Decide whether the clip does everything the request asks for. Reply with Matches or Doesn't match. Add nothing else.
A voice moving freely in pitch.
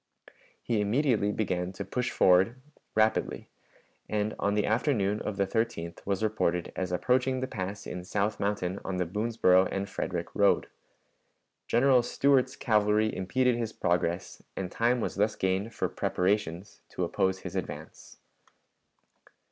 Doesn't match